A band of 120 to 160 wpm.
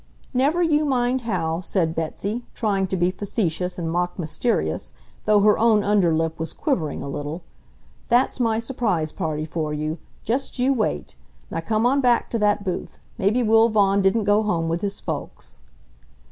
No: average, 175 wpm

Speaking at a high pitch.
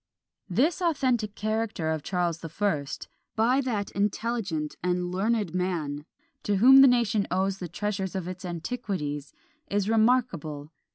Yes: high, 195 Hz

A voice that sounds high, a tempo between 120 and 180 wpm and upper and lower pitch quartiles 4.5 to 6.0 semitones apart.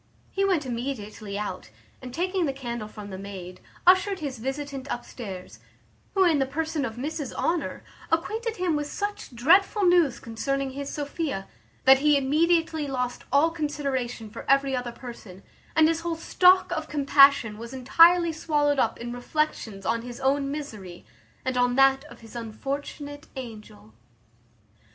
Yes: very high, 275 Hz; average, 155 wpm; average, 5.0 semitones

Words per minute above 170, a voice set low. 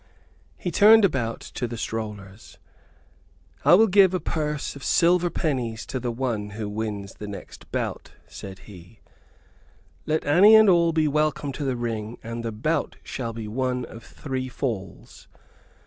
No: average, 160 wpm; low, 125 Hz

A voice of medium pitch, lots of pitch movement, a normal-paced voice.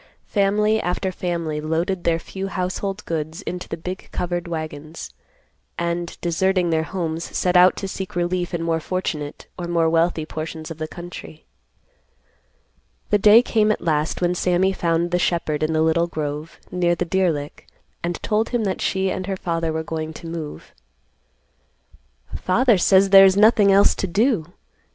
No: medium, 175 Hz; average, 2.8 semitones; average, 170 wpm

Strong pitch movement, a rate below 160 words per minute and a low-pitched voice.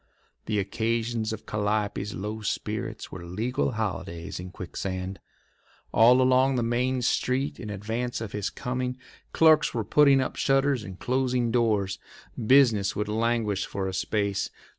No: average, 3.9 semitones; average, 140 wpm; low, 110 Hz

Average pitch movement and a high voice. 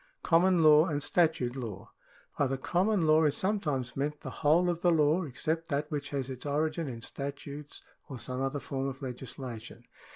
No: average, 3.3 semitones; medium, 145 Hz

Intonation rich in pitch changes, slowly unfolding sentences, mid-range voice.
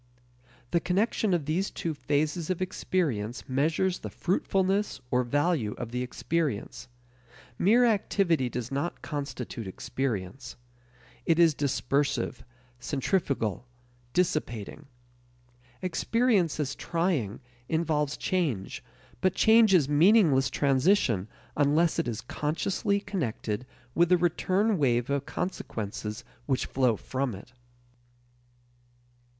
Yes: wide, 6.3 semitones; slow, 105 wpm; medium, 150 Hz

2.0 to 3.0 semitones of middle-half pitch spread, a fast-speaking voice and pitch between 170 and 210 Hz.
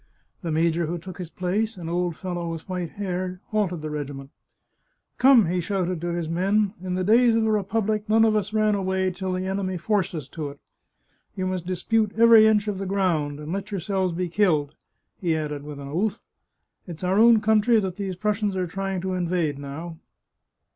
No: average, 3.5 semitones; fast, 210 wpm; medium, 185 Hz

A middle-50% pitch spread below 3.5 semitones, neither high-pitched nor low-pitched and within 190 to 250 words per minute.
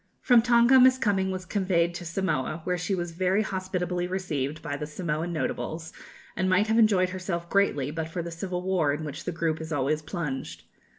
Yes: average, 3.0 semitones; medium, 180 Hz; average, 195 wpm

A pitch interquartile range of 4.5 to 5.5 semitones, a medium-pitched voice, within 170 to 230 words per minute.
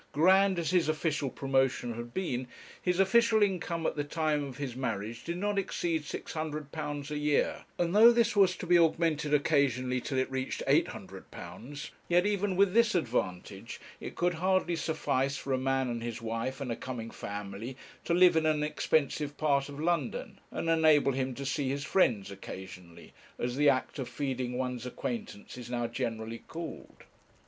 Yes: average, 5.1 semitones; medium, 145 Hz; average, 175 wpm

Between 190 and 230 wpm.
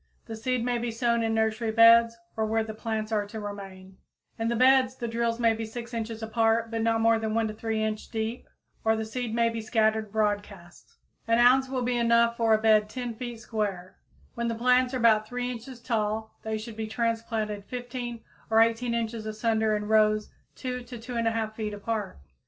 Yes: fast, 205 wpm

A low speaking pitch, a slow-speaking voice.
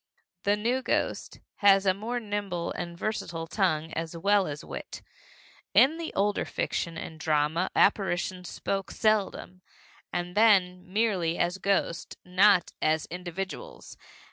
No: medium, 185 Hz; slow, 130 wpm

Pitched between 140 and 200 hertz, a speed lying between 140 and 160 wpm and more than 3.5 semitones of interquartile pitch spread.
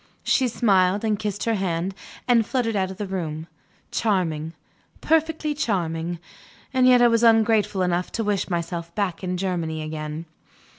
Yes: high, 190 Hz; average, 155 wpm; average, 5.0 semitones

